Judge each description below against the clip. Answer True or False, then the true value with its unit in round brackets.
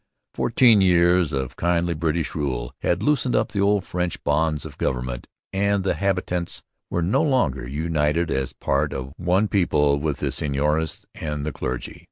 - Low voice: True (80 Hz)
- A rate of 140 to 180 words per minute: True (160 wpm)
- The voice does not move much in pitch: False (4.2 semitones)